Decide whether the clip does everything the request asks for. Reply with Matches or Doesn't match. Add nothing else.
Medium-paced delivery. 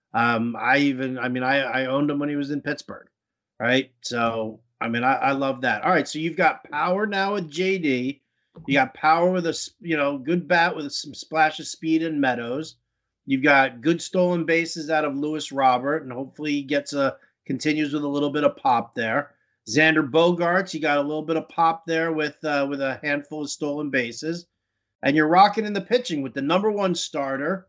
Doesn't match